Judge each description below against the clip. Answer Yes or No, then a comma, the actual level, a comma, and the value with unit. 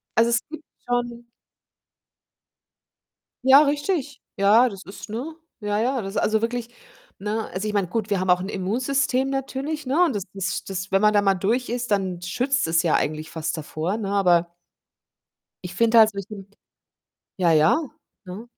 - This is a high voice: Yes, high, 210 Hz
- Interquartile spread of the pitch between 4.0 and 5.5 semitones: Yes, average, 4.7 semitones